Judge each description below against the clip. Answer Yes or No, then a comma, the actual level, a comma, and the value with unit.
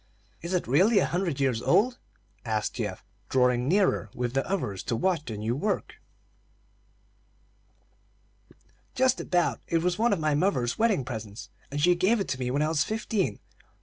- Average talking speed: Yes, average, 170 wpm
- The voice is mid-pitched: Yes, medium, 150 Hz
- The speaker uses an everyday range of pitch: No, wide, 7.5 semitones